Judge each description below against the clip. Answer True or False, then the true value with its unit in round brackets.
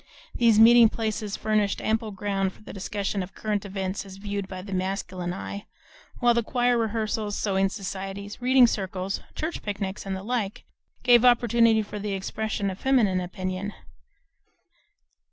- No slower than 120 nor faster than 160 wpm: True (150 wpm)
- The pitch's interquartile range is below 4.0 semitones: True (2.6 semitones)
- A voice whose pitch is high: True (205 Hz)